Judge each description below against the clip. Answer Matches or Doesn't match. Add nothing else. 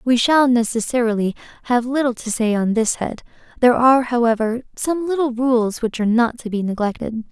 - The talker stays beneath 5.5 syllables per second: Doesn't match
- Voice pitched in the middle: Doesn't match